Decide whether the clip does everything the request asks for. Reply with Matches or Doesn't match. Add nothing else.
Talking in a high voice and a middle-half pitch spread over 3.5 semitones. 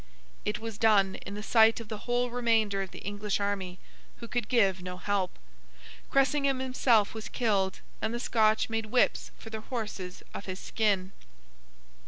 Doesn't match